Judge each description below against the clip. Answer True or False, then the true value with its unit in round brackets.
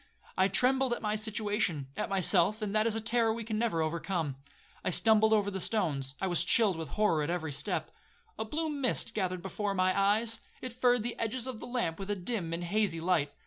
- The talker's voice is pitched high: True (205 Hz)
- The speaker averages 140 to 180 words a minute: False (205 wpm)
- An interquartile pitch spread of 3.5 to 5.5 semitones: True (4.4 semitones)